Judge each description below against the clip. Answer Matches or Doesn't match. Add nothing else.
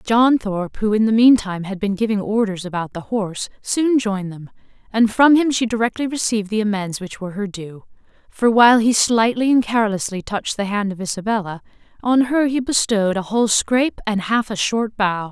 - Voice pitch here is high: Matches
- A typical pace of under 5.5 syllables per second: Doesn't match